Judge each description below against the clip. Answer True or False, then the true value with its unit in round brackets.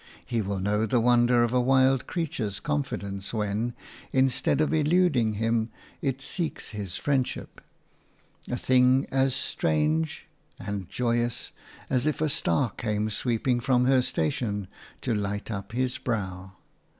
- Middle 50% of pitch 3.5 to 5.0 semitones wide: True (4.3 semitones)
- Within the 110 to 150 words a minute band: True (140 wpm)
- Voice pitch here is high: False (120 Hz)